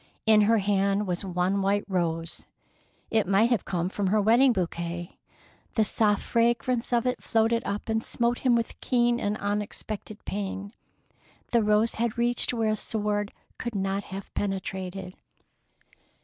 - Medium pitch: No, high, 210 Hz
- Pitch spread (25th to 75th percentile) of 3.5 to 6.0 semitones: No, average, 3.0 semitones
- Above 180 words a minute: No, average, 150 wpm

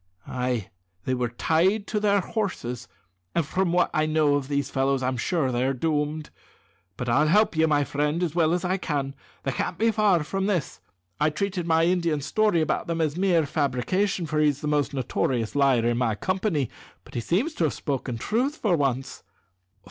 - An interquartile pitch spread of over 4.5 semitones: Yes, average, 5.0 semitones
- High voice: No, medium, 155 Hz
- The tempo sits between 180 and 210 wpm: Yes, average, 195 wpm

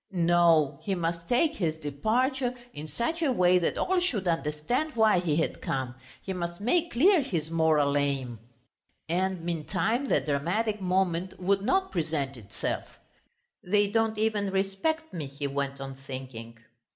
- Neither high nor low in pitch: Yes, medium, 175 Hz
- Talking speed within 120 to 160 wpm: Yes, average, 150 wpm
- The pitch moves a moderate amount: No, wide, 6.8 semitones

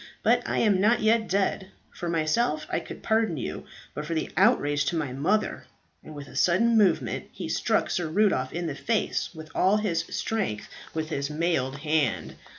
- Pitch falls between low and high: Yes, medium, 170 Hz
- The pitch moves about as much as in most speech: No, wide, 5.8 semitones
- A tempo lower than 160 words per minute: No, average, 190 wpm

